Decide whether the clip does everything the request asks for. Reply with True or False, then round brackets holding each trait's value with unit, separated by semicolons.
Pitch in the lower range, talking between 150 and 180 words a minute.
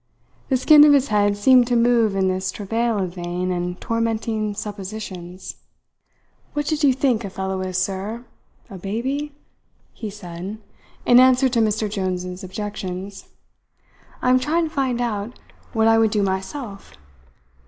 False (215 Hz; 155 wpm)